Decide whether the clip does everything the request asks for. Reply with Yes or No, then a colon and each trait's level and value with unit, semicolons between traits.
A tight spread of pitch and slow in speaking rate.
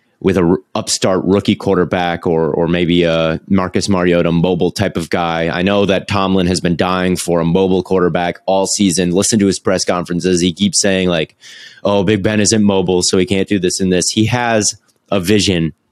No: narrow, 2.3 semitones; fast, 205 wpm